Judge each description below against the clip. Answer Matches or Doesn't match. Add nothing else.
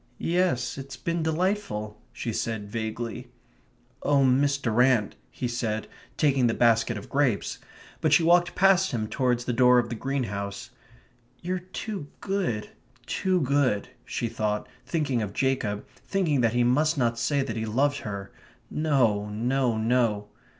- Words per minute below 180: Matches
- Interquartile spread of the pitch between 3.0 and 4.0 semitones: Doesn't match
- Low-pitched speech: Matches